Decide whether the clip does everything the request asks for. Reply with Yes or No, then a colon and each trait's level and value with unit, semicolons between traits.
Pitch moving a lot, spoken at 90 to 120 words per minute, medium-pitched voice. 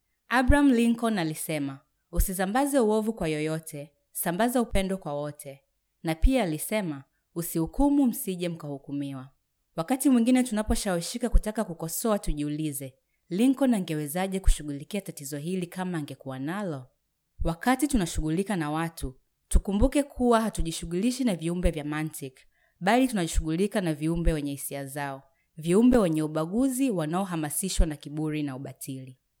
Yes: wide, 6.5 semitones; average, 115 wpm; medium, 170 Hz